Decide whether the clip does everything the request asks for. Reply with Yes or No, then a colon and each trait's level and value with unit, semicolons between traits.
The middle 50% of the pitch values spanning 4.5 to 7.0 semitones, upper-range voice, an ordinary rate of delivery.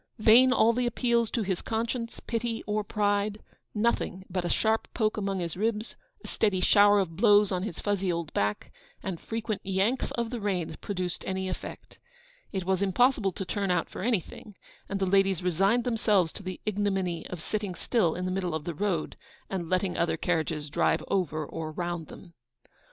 No: average, 3.3 semitones; high, 195 Hz; average, 185 wpm